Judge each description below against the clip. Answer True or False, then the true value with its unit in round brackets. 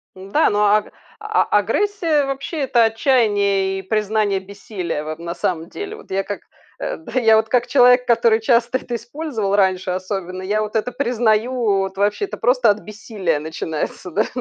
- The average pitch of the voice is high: True (215 Hz)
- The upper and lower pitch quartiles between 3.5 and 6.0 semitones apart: True (4.3 semitones)